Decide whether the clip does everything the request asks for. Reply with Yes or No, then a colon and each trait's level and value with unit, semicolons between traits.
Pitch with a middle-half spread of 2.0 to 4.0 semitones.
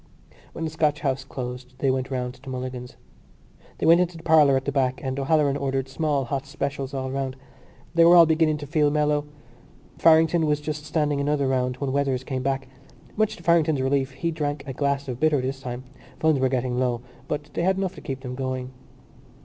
Yes: average, 2.8 semitones